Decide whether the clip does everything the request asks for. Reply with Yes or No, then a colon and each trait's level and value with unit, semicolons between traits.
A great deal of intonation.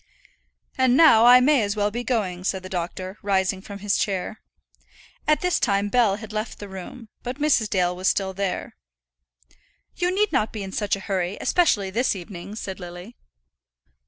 No: average, 4.2 semitones